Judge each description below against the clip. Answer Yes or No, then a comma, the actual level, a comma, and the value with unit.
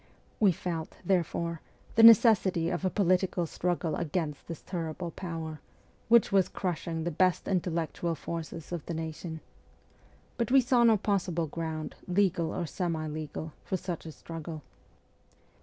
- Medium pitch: Yes, medium, 170 Hz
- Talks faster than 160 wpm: No, average, 155 wpm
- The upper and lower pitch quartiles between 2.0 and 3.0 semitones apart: Yes, narrow, 2.6 semitones